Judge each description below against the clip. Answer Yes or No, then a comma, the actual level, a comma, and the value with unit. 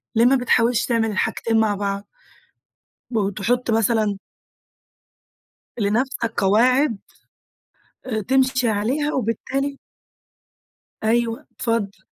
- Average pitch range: Yes, average, 3.2 semitones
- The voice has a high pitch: Yes, high, 230 Hz